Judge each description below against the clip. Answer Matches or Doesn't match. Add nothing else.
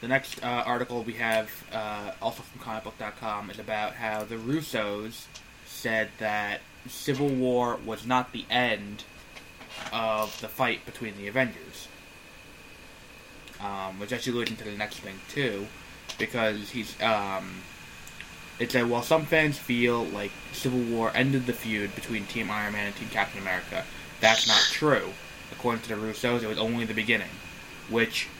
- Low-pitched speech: Matches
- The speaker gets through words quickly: Doesn't match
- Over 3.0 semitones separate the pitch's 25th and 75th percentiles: Doesn't match